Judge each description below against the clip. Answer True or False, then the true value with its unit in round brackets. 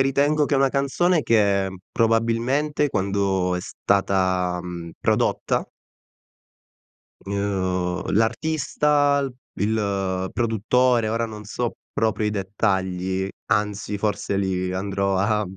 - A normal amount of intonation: True (4.2 semitones)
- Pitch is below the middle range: True (105 Hz)